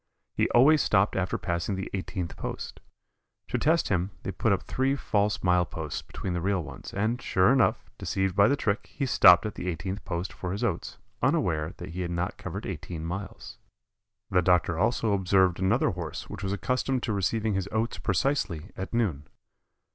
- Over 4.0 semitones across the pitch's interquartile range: No, average, 3.4 semitones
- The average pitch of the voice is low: Yes, very low, 95 Hz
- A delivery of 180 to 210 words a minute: Yes, average, 185 wpm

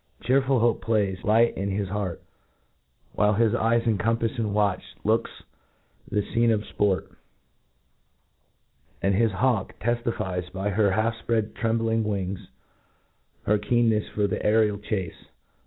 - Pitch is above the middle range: No, low, 110 Hz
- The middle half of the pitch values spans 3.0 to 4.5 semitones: No, narrow, 2.4 semitones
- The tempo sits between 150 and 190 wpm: No, average, 140 wpm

